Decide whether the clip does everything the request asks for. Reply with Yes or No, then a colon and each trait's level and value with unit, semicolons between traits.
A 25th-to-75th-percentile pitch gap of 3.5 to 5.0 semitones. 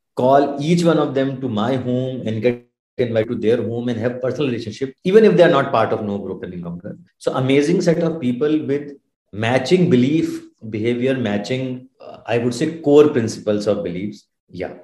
Yes: average, 4.1 semitones